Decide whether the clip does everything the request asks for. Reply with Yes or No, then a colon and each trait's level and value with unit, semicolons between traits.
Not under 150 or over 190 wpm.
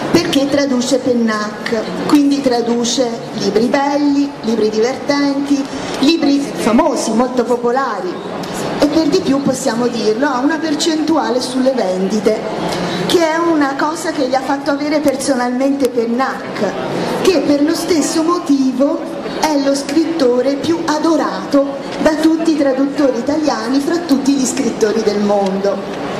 No: average, 130 wpm